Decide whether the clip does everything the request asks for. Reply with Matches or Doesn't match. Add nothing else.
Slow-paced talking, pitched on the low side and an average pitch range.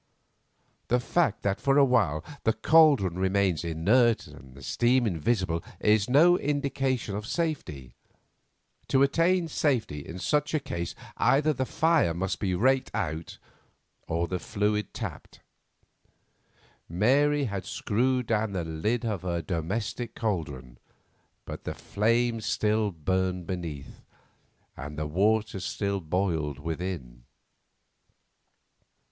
Doesn't match